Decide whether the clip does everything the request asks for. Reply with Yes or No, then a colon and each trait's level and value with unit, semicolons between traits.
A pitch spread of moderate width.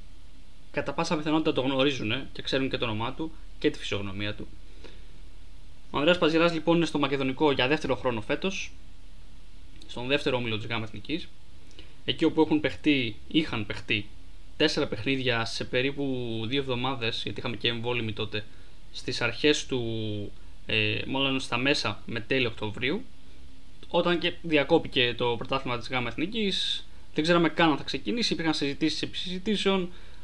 No: wide, 6.5 semitones